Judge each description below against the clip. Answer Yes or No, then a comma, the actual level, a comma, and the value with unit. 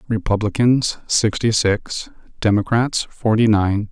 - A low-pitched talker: Yes, low, 110 Hz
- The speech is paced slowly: Yes, slow, 90 wpm